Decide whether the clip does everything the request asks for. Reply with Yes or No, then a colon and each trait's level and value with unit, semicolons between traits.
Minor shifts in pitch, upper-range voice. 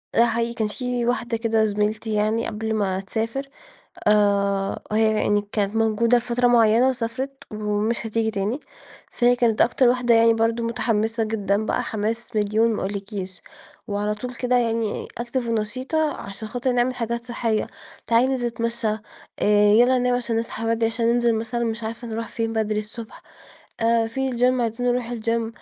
Yes: narrow, 2.0 semitones; high, 230 Hz